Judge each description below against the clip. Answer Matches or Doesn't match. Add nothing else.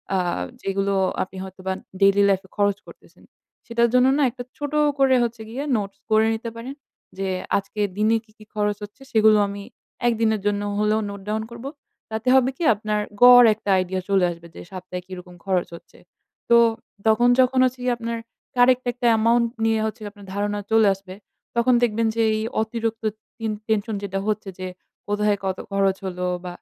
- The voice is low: Doesn't match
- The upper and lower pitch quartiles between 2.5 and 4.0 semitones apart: Matches